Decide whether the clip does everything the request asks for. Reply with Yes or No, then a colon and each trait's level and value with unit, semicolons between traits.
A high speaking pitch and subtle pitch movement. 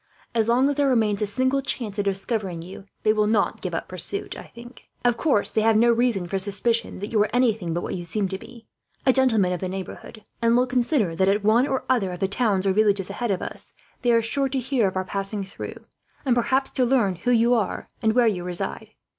No: high, 215 Hz; average, 4.1 semitones